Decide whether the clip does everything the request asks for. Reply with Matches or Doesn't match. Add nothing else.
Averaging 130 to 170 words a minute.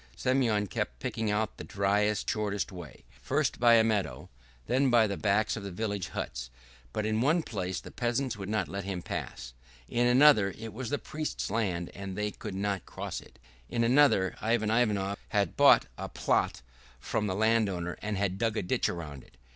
Doesn't match